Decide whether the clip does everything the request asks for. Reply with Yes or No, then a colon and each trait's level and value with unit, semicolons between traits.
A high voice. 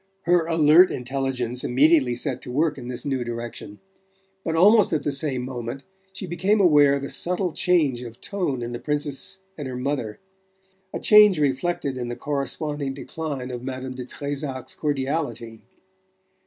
No: medium, 140 Hz